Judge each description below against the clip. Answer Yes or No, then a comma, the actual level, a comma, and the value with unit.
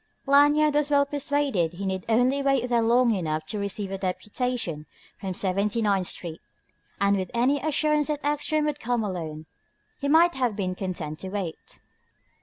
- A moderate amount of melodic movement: No, wide, 7.1 semitones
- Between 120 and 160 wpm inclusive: No, average, 170 wpm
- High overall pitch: Yes, high, 225 Hz